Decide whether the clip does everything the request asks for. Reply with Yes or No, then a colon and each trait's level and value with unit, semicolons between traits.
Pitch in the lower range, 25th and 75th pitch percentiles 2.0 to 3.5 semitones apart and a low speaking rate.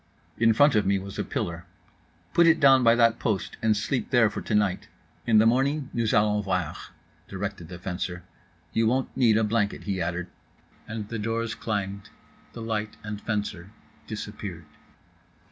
No: low, 105 Hz; average, 2.9 semitones; average, 165 wpm